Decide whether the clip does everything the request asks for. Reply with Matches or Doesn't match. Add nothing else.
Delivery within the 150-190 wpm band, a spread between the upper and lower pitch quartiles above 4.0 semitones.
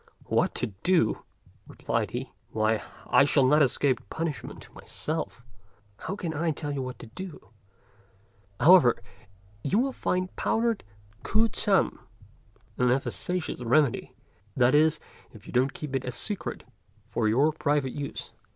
Doesn't match